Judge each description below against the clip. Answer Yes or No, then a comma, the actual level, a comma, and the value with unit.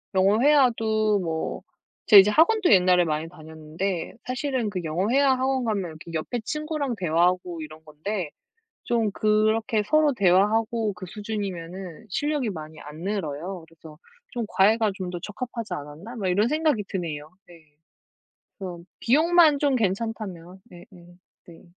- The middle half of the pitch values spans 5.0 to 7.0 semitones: Yes, average, 5.3 semitones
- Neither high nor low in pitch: No, high, 200 Hz